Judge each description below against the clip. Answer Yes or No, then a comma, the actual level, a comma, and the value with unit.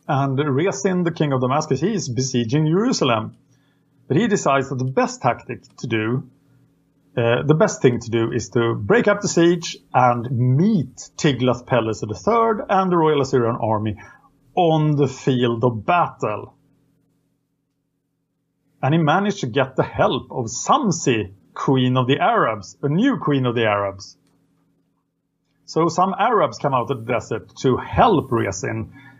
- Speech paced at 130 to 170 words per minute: Yes, average, 155 wpm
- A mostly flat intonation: No, average, 4.2 semitones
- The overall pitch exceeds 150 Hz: No, low, 135 Hz